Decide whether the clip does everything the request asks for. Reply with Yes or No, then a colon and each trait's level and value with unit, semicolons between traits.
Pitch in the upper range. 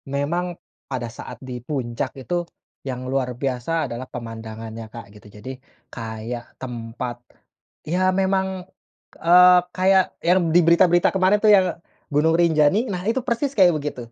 No: medium, 145 Hz